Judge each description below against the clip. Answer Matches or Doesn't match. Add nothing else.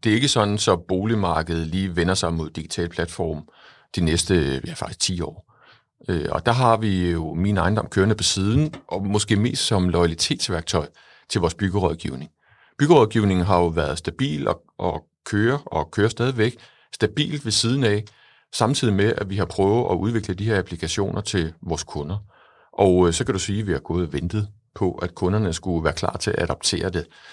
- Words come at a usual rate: Matches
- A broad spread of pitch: Doesn't match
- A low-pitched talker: Matches